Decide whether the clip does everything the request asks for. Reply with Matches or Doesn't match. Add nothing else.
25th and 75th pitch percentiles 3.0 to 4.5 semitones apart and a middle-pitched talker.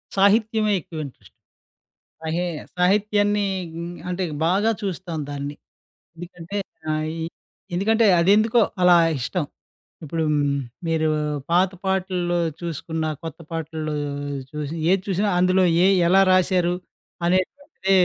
Matches